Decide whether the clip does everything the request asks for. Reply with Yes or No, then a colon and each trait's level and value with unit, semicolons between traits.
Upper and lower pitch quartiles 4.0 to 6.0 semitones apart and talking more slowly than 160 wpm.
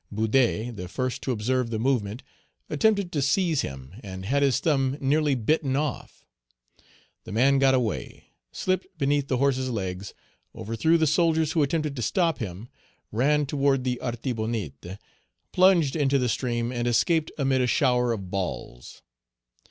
Yes: average, 4.3 semitones; average, 150 wpm